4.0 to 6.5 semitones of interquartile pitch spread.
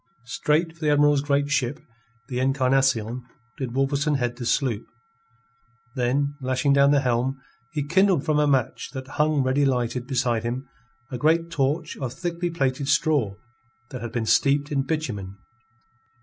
No: average, 2.8 semitones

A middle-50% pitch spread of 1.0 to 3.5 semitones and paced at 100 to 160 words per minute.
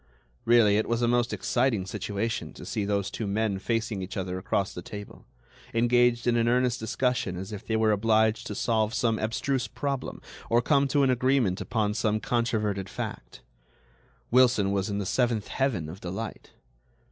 No: average, 3.1 semitones; average, 175 wpm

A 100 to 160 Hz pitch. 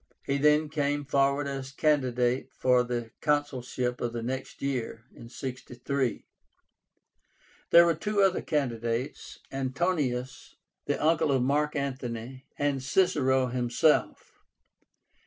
Yes: low, 135 Hz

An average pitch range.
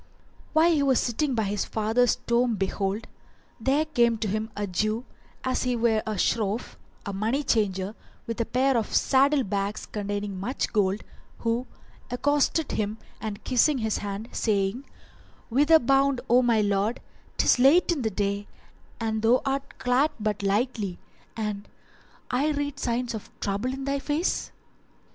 Yes: average, 4.3 semitones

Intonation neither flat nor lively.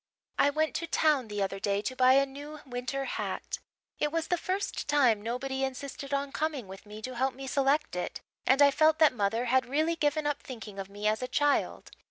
Yes: average, 3.9 semitones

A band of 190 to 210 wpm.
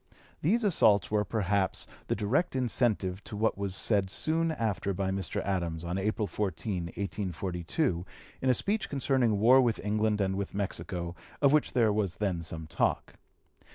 No: average, 160 wpm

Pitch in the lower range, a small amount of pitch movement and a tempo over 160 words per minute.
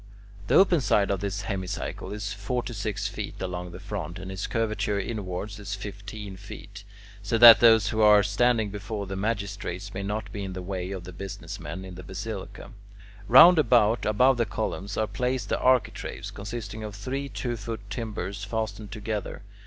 Yes: low, 105 Hz; narrow, 2.3 semitones; average, 180 wpm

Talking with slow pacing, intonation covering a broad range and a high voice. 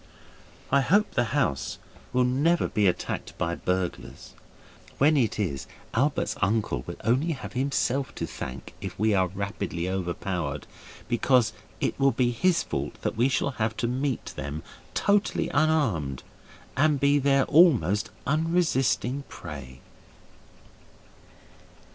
No: slow, 130 wpm; wide, 7.3 semitones; low, 120 Hz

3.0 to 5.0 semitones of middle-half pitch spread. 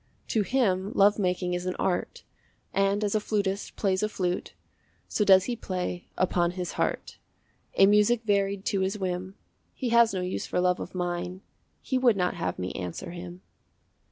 No: narrow, 2.5 semitones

